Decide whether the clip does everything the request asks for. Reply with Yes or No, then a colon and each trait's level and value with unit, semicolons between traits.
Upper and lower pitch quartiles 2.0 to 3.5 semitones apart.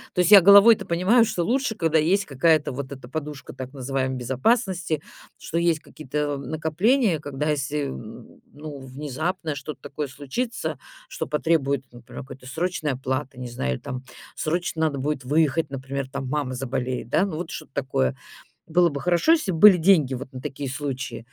No: average, 4.3 semitones